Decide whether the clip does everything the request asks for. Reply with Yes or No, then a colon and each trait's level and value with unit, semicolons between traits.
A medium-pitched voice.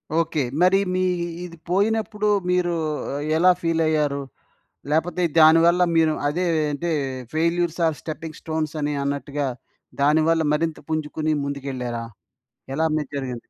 Yes: medium, 160 Hz